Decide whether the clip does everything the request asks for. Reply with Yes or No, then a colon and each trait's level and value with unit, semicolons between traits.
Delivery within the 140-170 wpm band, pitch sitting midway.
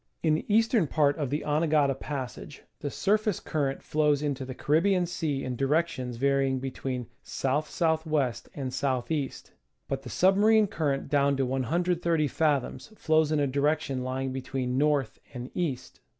Yes: average, 160 wpm; medium, 145 Hz